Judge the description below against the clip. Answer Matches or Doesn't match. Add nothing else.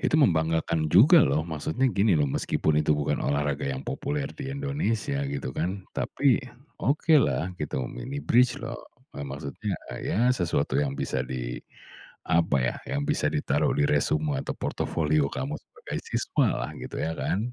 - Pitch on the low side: Matches